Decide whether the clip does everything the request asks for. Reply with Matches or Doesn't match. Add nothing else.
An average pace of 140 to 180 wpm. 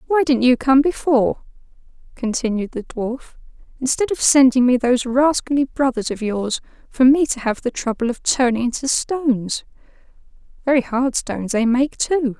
Matches